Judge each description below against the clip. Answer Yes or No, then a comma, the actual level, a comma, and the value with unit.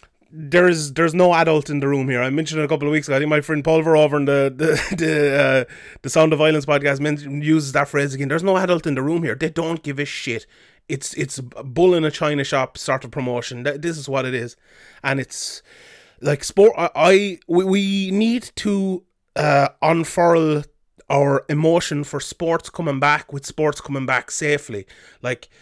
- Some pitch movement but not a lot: Yes, average, 3.0 semitones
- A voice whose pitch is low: No, medium, 150 Hz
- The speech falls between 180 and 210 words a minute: Yes, fast, 205 wpm